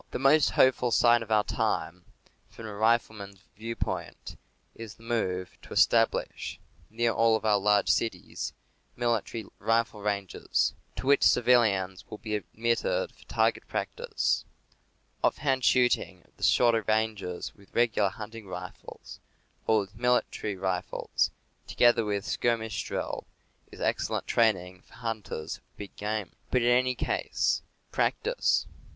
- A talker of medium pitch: No, low, 110 Hz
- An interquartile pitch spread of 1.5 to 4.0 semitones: Yes, average, 2.8 semitones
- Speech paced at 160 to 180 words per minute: No, slow, 135 wpm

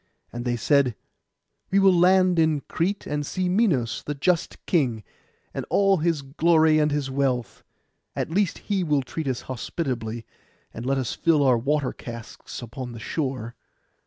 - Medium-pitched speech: Yes, medium, 145 Hz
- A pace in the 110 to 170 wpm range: Yes, average, 160 wpm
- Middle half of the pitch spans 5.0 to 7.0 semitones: Yes, average, 5.3 semitones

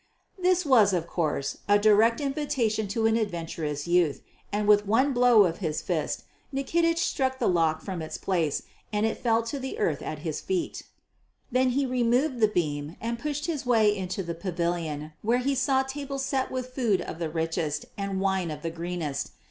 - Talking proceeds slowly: No, average, 190 wpm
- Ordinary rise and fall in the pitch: No, wide, 7.4 semitones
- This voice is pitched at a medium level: No, high, 215 Hz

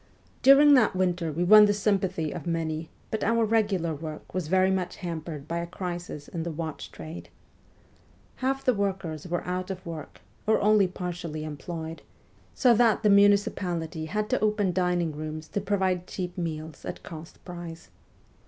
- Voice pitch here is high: No, medium, 180 Hz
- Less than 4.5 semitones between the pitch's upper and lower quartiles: Yes, average, 3.8 semitones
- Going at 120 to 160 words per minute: No, average, 170 wpm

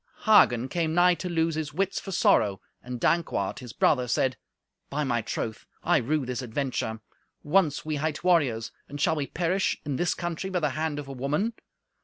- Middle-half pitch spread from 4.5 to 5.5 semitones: Yes, average, 5.2 semitones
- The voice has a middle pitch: Yes, medium, 150 Hz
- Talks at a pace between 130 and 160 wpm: No, average, 190 wpm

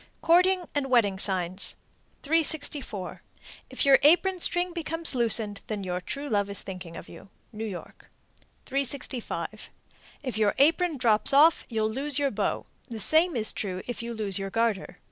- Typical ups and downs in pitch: No, wide, 6.6 semitones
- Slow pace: No, average, 160 wpm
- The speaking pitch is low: No, high, 235 Hz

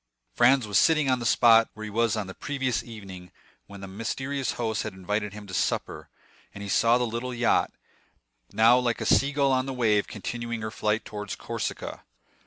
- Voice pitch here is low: Yes, low, 115 Hz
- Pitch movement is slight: No, average, 3.3 semitones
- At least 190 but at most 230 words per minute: Yes, average, 195 wpm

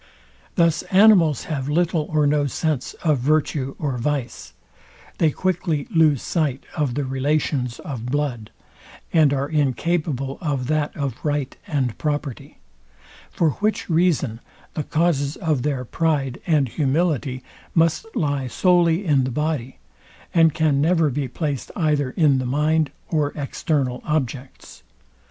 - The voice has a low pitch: No, medium, 145 Hz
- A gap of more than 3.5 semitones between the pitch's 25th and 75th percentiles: No, average, 3.1 semitones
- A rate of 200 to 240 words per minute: No, slow, 135 wpm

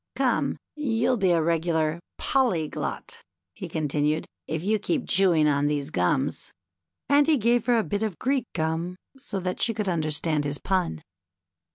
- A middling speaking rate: Yes, average, 170 wpm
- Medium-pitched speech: Yes, medium, 175 Hz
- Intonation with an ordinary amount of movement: No, wide, 6.5 semitones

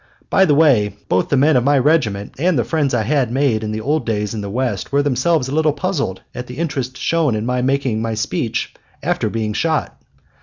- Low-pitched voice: Yes, low, 130 Hz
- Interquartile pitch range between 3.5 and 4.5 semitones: No, average, 5.0 semitones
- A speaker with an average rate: No, fast, 225 wpm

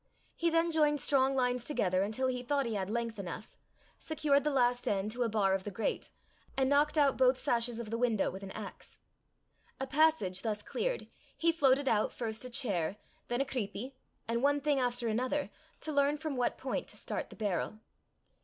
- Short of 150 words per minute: No, average, 200 wpm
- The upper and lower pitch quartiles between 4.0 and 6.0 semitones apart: Yes, average, 4.7 semitones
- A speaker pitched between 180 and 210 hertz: No, very high, 250 Hz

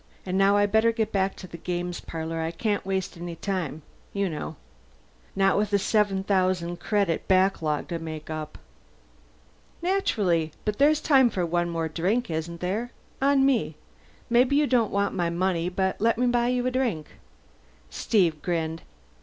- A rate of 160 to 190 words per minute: Yes, average, 170 wpm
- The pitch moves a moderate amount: Yes, average, 4.7 semitones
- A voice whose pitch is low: No, high, 190 Hz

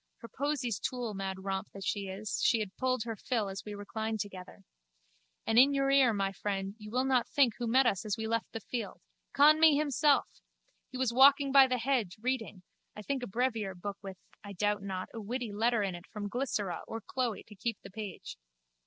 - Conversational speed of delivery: No, fast, 210 wpm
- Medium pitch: No, high, 225 Hz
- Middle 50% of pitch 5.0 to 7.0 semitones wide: No, average, 4.3 semitones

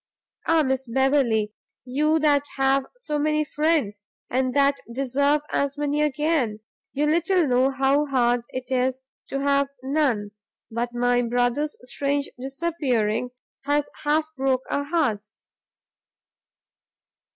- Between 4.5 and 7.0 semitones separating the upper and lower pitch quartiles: No, average, 3.0 semitones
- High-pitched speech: Yes, very high, 275 Hz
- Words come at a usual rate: No, slow, 130 wpm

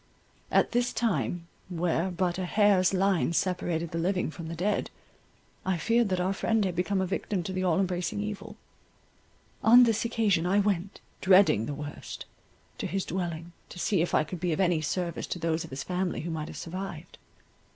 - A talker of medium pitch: Yes, medium, 180 Hz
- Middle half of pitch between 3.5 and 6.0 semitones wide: No, average, 2.7 semitones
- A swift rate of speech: No, average, 195 wpm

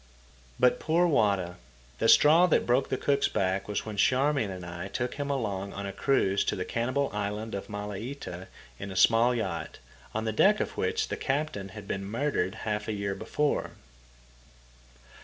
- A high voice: No, low, 110 Hz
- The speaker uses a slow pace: No, average, 175 wpm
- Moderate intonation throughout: No, wide, 5.8 semitones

